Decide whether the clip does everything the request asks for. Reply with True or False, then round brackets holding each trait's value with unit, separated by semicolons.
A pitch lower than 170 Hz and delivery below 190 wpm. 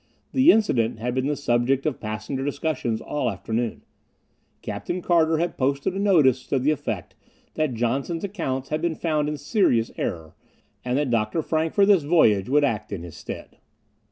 True (140 Hz; 175 wpm)